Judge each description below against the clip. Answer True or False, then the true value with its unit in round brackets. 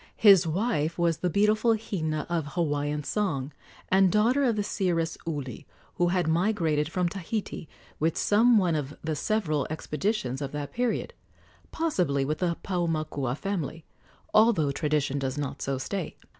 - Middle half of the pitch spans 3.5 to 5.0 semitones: False (5.4 semitones)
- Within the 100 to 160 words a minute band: True (150 wpm)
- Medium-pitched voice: True (165 Hz)